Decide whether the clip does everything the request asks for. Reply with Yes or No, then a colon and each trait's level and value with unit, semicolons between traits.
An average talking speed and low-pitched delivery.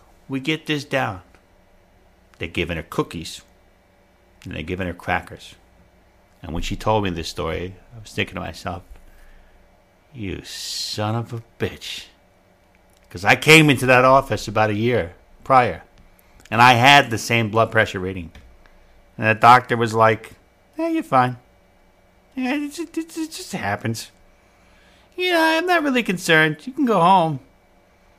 Yes: average, 145 wpm; low, 100 Hz